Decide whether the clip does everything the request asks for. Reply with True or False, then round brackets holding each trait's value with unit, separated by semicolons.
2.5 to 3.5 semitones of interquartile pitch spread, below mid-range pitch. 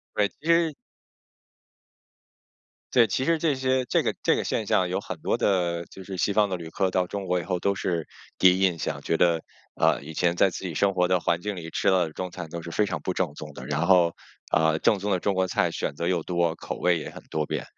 True (2.8 semitones; 90 Hz)